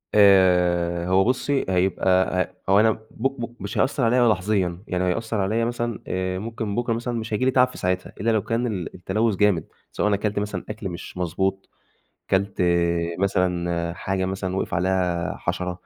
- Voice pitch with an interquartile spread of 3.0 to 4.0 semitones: Yes, average, 3.6 semitones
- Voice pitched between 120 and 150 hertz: No, very low, 95 Hz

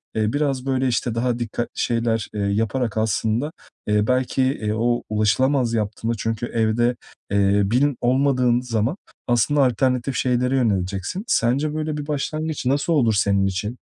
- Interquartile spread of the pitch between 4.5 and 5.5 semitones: No, average, 3.3 semitones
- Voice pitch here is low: Yes, low, 120 Hz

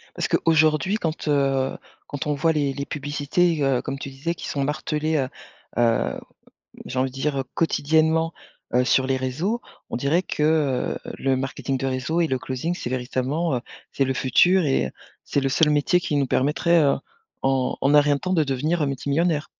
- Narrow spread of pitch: No, average, 3.1 semitones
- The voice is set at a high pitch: No, medium, 145 Hz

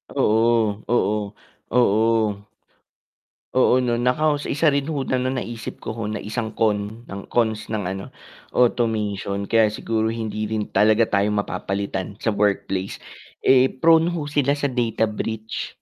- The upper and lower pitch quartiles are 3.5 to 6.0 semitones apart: No, average, 3.0 semitones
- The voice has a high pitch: No, low, 110 Hz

